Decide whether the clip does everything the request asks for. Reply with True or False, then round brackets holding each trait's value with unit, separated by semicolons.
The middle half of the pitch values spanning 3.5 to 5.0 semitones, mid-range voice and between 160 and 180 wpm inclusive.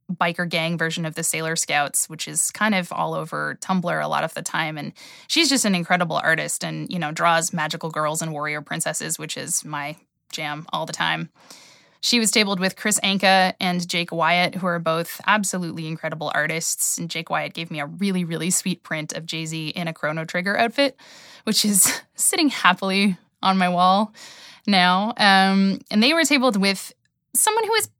False (3.8 semitones; 180 Hz; 195 wpm)